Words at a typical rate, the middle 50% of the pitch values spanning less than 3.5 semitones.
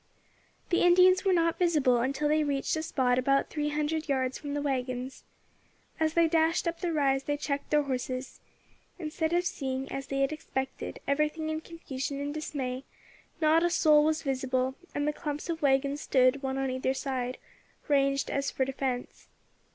Yes: average, 175 wpm; average, 2.9 semitones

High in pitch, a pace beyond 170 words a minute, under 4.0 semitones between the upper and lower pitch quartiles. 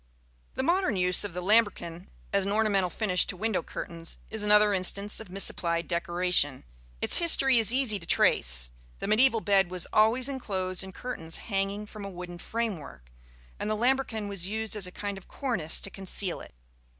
Yes: high, 200 Hz; average, 180 wpm; average, 3.5 semitones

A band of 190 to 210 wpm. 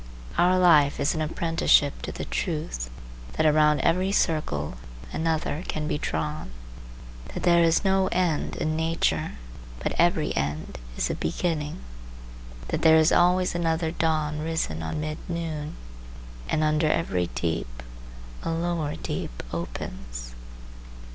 No: slow, 135 wpm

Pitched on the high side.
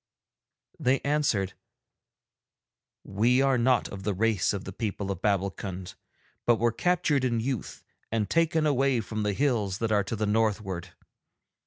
No: low, 110 Hz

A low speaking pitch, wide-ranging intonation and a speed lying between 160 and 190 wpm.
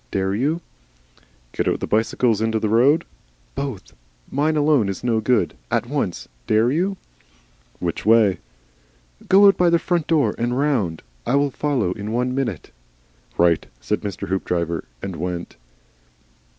No: low, 115 Hz; wide, 6.7 semitones; average, 150 wpm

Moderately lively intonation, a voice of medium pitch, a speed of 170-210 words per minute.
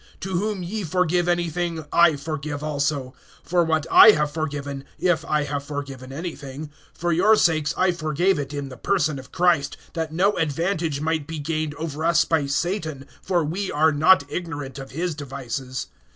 Yes: average, 3.3 semitones; medium, 155 Hz; average, 175 wpm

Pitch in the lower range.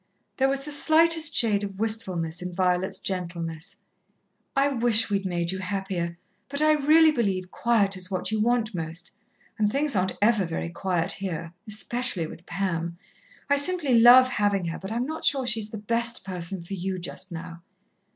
No: high, 200 Hz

